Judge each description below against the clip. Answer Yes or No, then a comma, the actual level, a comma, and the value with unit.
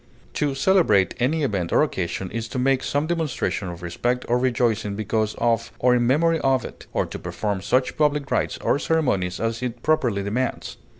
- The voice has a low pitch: Yes, low, 125 Hz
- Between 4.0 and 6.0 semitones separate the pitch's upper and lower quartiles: Yes, average, 5.1 semitones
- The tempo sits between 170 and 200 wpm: Yes, average, 185 wpm